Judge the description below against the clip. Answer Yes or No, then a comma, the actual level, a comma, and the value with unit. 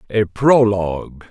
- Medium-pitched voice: No, low, 105 Hz